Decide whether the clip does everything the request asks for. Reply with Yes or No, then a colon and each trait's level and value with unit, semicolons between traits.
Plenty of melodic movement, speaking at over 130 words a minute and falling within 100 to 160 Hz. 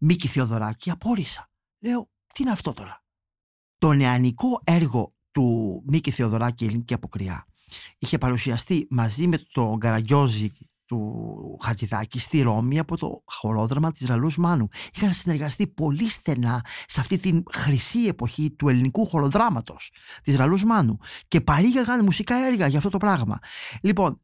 Yes: wide, 6.8 semitones; average, 140 wpm; medium, 140 Hz